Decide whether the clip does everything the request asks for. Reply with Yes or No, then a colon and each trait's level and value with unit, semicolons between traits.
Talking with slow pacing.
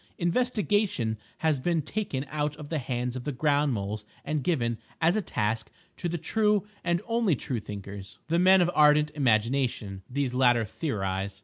No: average, 170 wpm